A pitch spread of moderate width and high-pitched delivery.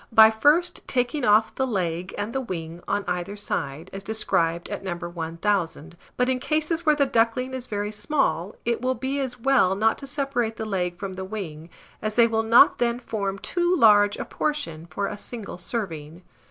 No: wide, 5.8 semitones; high, 215 Hz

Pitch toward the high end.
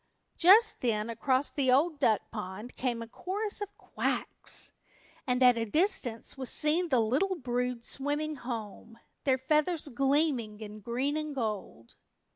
Yes: very high, 260 Hz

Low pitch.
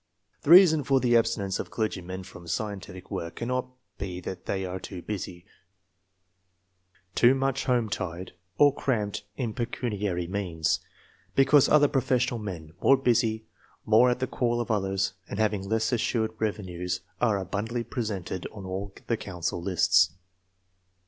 Yes: low, 105 Hz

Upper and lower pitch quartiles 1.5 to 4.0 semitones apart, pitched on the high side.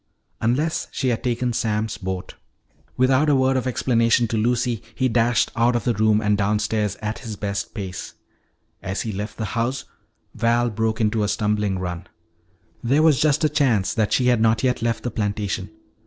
No: average, 2.9 semitones; low, 115 Hz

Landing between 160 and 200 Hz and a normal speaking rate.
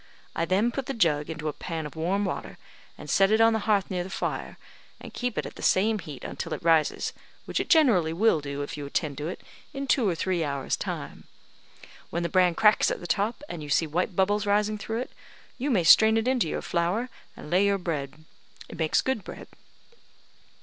No: medium, 185 Hz; fast, 220 wpm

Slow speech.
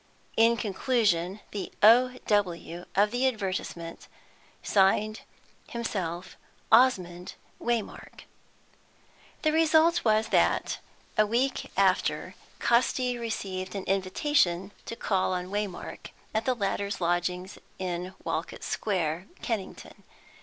Yes: slow, 105 wpm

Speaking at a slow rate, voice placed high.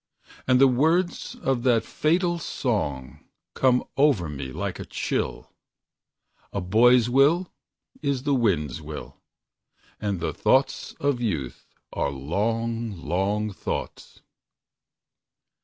No: slow, 110 wpm; low, 115 Hz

